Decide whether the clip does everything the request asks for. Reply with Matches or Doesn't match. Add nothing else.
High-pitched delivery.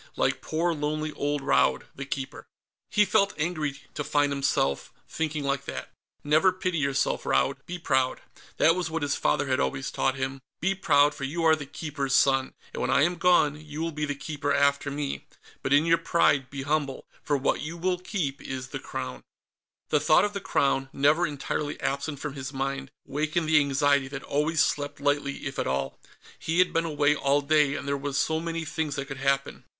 Doesn't match